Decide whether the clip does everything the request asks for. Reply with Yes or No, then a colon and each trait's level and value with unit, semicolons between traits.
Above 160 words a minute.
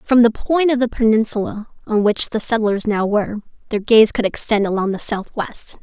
Yes: average, 195 wpm